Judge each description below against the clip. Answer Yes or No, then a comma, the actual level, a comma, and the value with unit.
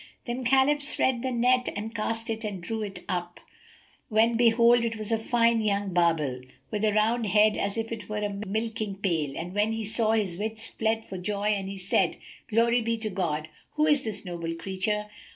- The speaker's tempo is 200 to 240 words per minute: Yes, fast, 205 wpm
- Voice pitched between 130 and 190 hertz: No, high, 215 Hz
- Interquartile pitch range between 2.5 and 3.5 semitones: Yes, average, 2.9 semitones